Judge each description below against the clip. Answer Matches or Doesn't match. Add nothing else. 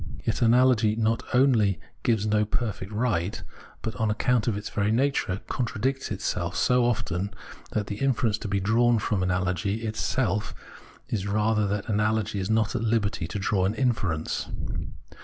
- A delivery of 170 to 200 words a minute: Doesn't match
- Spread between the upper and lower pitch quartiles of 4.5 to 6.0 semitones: Doesn't match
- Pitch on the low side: Matches